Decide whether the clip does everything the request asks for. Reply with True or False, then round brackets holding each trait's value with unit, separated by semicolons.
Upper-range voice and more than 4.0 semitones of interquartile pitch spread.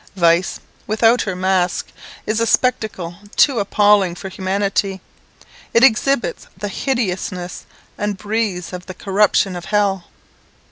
False (200 Hz; 2.8 semitones)